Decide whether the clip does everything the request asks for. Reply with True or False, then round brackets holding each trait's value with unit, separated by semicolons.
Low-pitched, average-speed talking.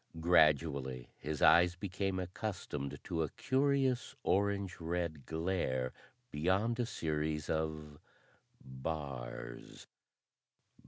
False (80 Hz; 90 wpm)